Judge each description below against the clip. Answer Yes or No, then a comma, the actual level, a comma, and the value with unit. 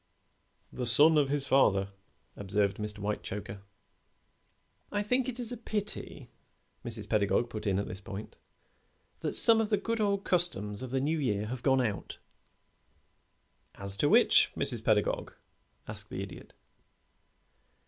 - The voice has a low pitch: Yes, low, 125 Hz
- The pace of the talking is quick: No, average, 145 wpm